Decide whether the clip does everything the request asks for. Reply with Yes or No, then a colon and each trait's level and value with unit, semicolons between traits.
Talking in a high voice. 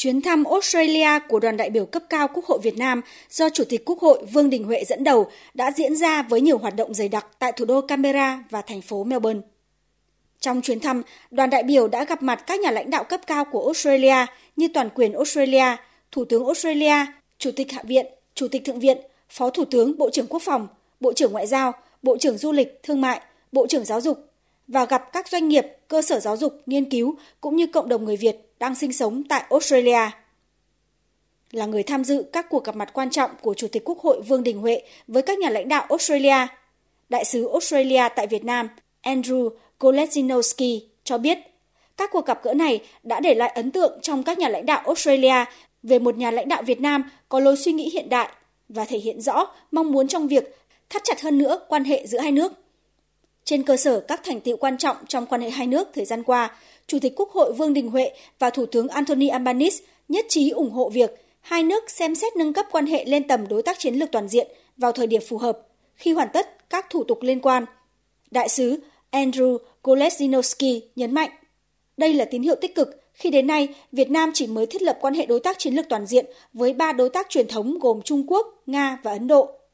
Yes: very high, 270 Hz